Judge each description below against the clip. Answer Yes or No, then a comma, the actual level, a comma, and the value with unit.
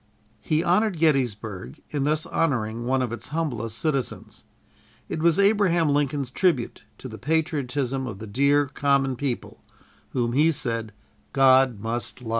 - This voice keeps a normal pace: Yes, average, 145 wpm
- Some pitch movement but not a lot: Yes, average, 4.6 semitones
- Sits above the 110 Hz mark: Yes, low, 135 Hz